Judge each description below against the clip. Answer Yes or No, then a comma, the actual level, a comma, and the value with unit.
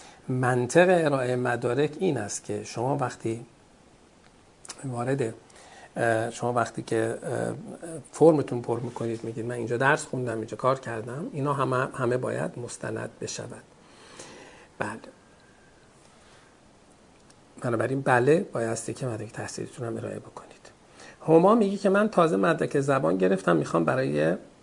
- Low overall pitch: Yes, low, 125 Hz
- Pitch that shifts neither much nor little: Yes, average, 4.4 semitones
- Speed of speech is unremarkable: Yes, average, 120 wpm